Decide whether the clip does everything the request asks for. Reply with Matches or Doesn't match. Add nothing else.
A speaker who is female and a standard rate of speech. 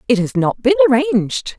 Matches